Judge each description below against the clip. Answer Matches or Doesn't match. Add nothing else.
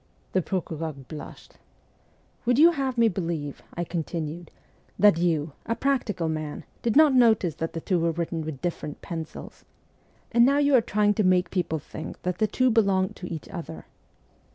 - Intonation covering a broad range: Matches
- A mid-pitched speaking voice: Matches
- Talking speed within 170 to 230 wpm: Matches